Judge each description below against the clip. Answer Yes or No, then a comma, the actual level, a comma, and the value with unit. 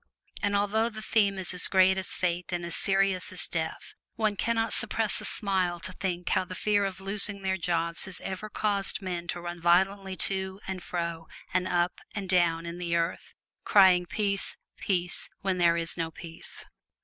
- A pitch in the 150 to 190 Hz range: Yes, medium, 185 Hz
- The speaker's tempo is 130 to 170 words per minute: No, average, 190 wpm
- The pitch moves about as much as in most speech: No, narrow, 2.3 semitones